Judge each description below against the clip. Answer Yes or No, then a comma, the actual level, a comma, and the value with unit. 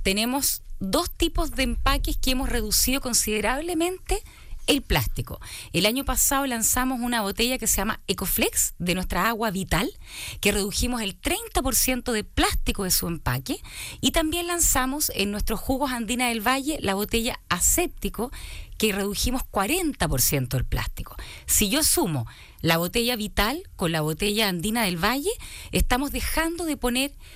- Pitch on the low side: No, high, 235 Hz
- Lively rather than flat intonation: Yes, wide, 5.7 semitones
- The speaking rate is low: No, average, 145 wpm